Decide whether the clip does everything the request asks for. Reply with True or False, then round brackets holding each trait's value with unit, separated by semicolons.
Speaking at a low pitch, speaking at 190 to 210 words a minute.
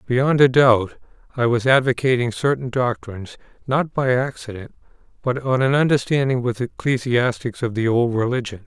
False (125 Hz; 145 wpm)